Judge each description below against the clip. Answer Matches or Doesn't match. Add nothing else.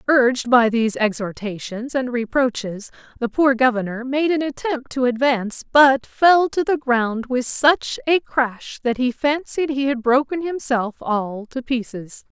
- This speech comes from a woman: Matches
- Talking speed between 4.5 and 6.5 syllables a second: Doesn't match